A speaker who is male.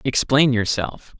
Yes: male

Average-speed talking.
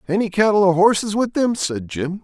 No: fast, 215 wpm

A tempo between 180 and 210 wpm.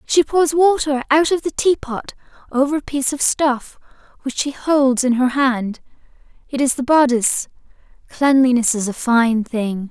No: average, 165 wpm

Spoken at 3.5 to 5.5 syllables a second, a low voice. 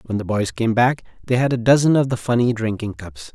No: 5.8 syllables/s; low, 115 Hz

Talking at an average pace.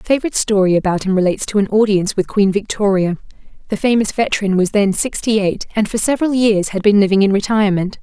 No: fast, 210 wpm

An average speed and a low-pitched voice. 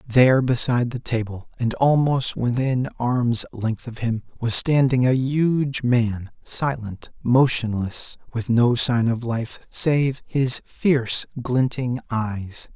No: slow, 130 wpm; low, 125 Hz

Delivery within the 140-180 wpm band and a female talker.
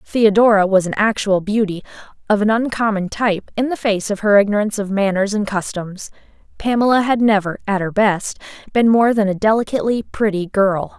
Yes: average, 175 wpm; female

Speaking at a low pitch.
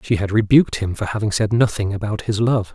Yes: low, 105 Hz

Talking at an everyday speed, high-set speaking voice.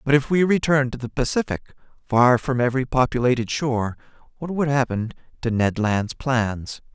No: average, 165 wpm; low, 125 Hz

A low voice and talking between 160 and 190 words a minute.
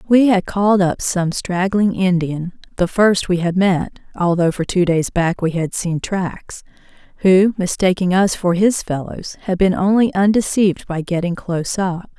No: medium, 185 Hz; average, 165 wpm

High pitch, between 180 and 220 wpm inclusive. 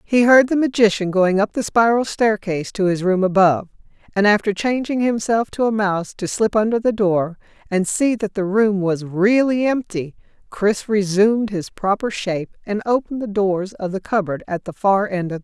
Yes: high, 205 Hz; average, 200 wpm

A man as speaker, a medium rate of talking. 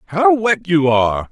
Yes: male; average, 180 wpm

